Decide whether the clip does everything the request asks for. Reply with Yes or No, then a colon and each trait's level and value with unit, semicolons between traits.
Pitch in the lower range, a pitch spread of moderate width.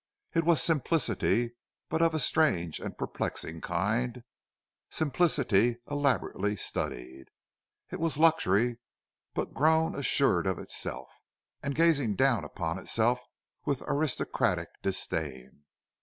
No: low, 125 Hz; wide, 8.3 semitones